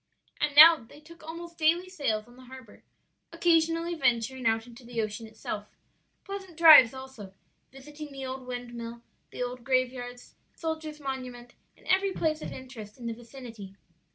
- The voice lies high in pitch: Yes, very high, 260 Hz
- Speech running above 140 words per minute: Yes, average, 160 wpm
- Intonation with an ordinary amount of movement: Yes, average, 5.0 semitones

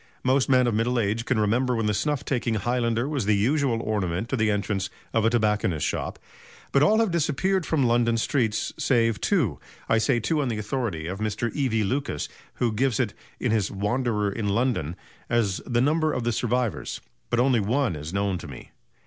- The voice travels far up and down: No, average, 3.7 semitones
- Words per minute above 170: Yes, average, 200 wpm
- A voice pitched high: No, low, 115 Hz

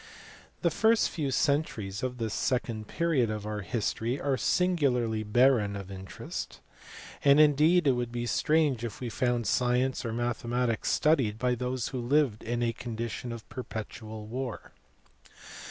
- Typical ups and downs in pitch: Yes, average, 3.5 semitones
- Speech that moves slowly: No, average, 150 wpm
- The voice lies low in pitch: Yes, low, 120 Hz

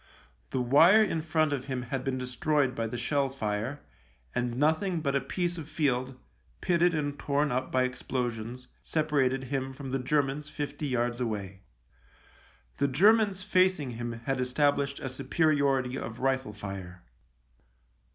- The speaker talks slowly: No, average, 150 wpm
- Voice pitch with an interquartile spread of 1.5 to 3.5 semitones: Yes, average, 3.2 semitones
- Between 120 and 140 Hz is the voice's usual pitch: Yes, low, 135 Hz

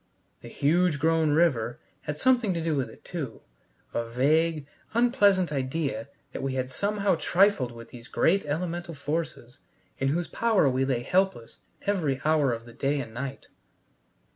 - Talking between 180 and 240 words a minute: No, average, 160 wpm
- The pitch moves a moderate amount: Yes, average, 5.0 semitones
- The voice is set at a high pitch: No, medium, 150 Hz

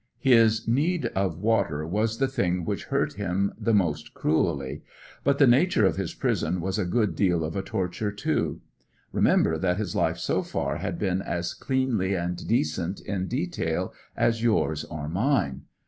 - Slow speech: No, average, 170 wpm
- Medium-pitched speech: No, very low, 95 Hz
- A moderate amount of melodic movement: Yes, average, 5.0 semitones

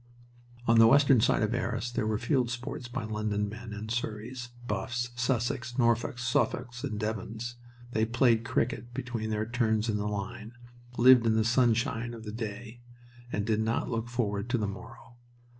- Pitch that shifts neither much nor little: No, narrow, 1.9 semitones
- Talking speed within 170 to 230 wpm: Yes, average, 175 wpm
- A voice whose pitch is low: Yes, low, 115 Hz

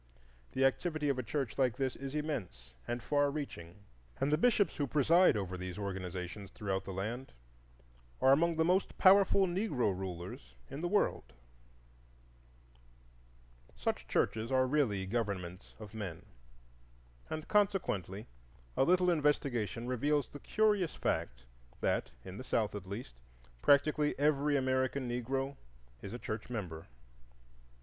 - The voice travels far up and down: Yes, wide, 7.0 semitones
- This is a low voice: Yes, low, 130 Hz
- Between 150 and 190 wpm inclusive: No, slow, 135 wpm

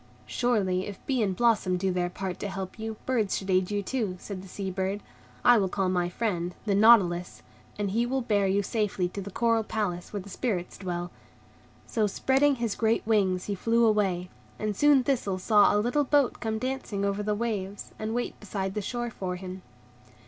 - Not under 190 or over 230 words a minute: Yes, average, 200 wpm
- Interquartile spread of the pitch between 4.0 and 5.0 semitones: No, average, 3.4 semitones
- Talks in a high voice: Yes, high, 205 Hz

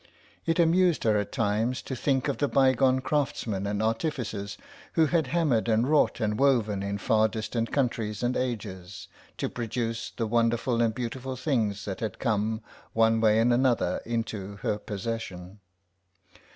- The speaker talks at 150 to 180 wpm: Yes, average, 155 wpm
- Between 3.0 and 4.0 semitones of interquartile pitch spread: Yes, average, 3.5 semitones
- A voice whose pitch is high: No, low, 115 Hz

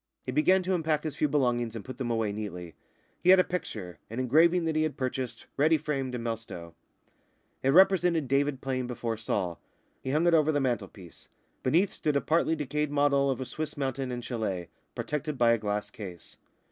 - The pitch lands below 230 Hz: Yes, low, 135 Hz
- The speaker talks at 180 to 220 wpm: Yes, average, 195 wpm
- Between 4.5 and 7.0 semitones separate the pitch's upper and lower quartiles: Yes, average, 5.0 semitones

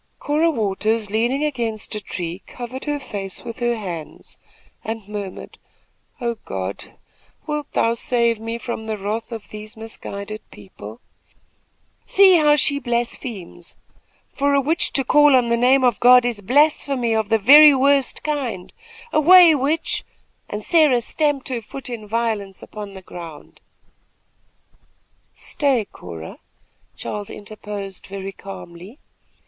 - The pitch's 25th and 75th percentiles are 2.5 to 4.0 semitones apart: No, average, 5.0 semitones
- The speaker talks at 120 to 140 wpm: Yes, slow, 135 wpm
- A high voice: Yes, high, 230 Hz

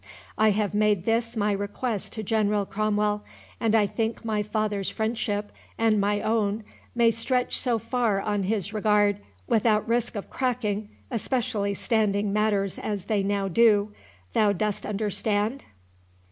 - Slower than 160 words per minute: Yes, average, 140 wpm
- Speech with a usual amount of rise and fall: No, narrow, 1.7 semitones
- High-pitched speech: Yes, high, 210 Hz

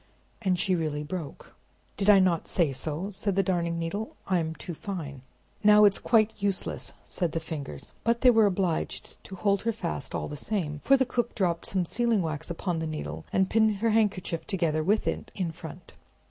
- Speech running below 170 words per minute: No, average, 195 wpm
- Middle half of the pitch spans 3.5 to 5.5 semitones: Yes, average, 4.1 semitones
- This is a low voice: No, medium, 185 Hz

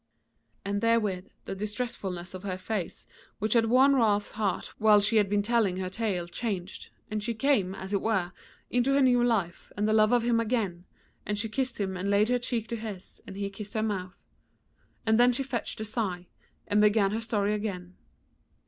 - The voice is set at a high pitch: Yes, high, 210 Hz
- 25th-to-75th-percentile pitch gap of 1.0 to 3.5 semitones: Yes, average, 2.9 semitones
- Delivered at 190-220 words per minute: Yes, average, 200 wpm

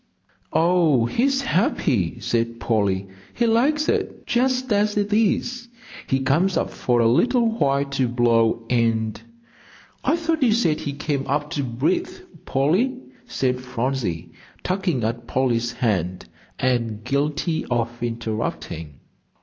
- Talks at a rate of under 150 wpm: Yes, slow, 135 wpm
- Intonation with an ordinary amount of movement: No, wide, 8.8 semitones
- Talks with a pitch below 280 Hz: Yes, low, 135 Hz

